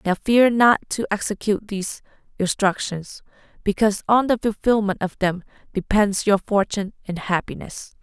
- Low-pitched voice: No, high, 205 Hz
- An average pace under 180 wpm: Yes, slow, 135 wpm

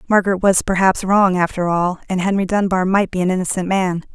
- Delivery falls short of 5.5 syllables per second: No, 5.8 syllables/s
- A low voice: No, medium, 185 Hz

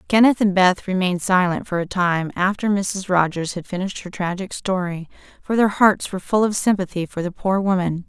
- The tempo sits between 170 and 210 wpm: Yes, average, 200 wpm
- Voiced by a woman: Yes, female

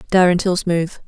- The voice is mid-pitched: Yes, medium, 180 Hz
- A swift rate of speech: No, average, 165 wpm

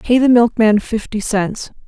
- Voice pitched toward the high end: Yes, high, 225 Hz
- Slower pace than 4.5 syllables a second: Yes, 4.2 syllables/s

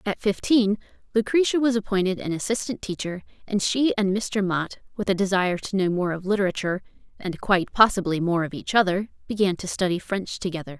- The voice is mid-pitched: No, high, 195 Hz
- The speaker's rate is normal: Yes, average, 185 wpm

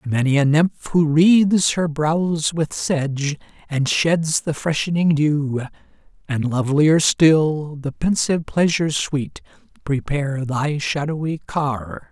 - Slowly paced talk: Yes, slow, 130 wpm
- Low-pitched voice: No, medium, 150 Hz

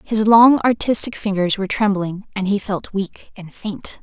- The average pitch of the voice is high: Yes, high, 205 Hz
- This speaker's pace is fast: No, average, 180 wpm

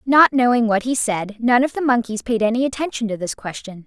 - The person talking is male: No, female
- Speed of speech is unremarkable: No, fast, 235 wpm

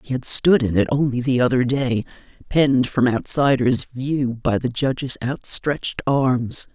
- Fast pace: No, average, 160 wpm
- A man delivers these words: No, female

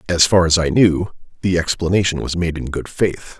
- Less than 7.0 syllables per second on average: Yes, 5.6 syllables/s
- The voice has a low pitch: Yes, very low, 85 Hz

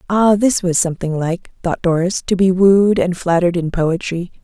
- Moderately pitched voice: Yes, medium, 180 Hz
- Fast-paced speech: No, average, 190 wpm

